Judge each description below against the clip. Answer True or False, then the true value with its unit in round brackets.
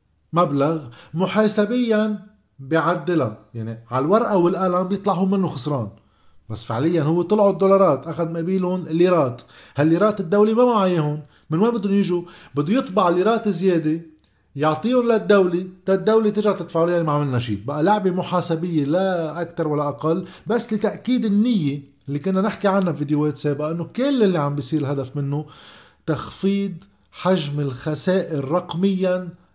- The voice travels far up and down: False (4.9 semitones)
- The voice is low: False (175 Hz)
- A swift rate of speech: True (140 wpm)